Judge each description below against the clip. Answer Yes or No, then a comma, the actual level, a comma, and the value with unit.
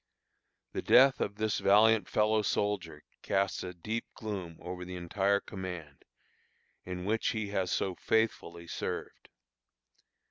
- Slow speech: Yes, slow, 130 wpm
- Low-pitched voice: Yes, low, 100 Hz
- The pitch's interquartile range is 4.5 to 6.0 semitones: No, average, 3.1 semitones